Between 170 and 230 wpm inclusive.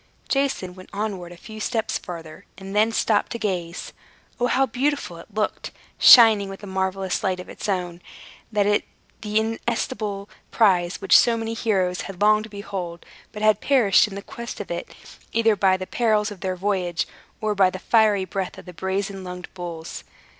Yes: average, 180 wpm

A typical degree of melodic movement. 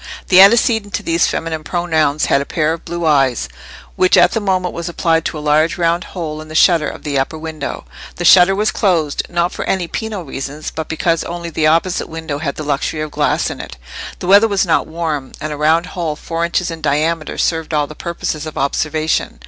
No: narrow, 2.3 semitones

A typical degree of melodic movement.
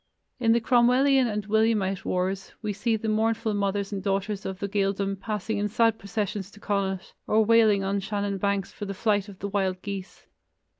No: narrow, 2.0 semitones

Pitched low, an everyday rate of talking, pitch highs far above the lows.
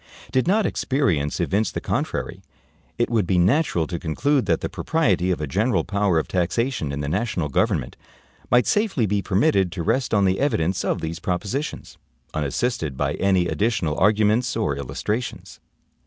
Yes: low, 100 Hz; average, 165 wpm; wide, 6.5 semitones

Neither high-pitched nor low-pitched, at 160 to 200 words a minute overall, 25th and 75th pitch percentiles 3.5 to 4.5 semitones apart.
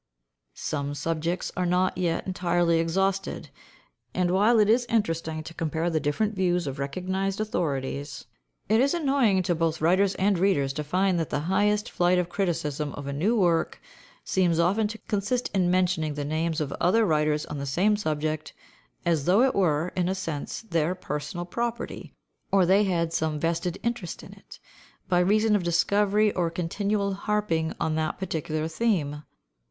Yes: medium, 175 Hz; average, 170 wpm; average, 3.9 semitones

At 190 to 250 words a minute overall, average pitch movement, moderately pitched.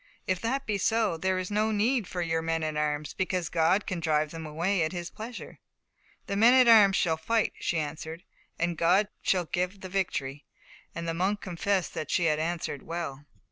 Yes: average, 195 wpm; average, 3.8 semitones; medium, 175 Hz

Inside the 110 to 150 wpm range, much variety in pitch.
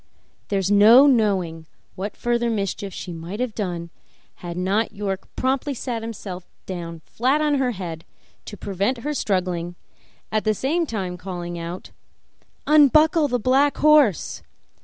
Yes: average, 145 wpm; wide, 6.0 semitones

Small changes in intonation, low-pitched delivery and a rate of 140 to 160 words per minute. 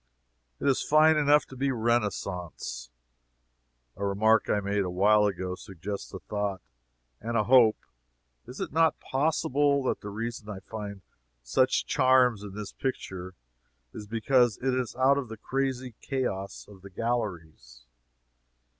No: average, 4.9 semitones; low, 110 Hz; average, 150 wpm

